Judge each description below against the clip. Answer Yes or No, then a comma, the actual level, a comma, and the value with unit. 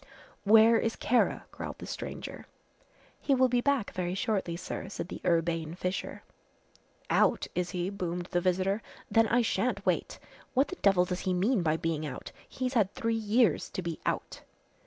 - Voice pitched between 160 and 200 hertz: Yes, high, 190 Hz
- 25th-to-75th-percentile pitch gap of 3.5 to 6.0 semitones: Yes, average, 4.4 semitones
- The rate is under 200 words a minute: Yes, average, 175 wpm